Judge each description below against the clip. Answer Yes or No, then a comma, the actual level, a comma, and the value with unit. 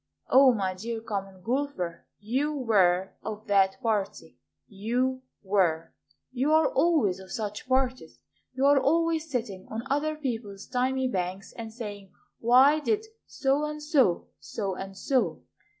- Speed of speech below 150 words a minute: Yes, average, 140 wpm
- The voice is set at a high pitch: Yes, high, 230 Hz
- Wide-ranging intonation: Yes, wide, 5.7 semitones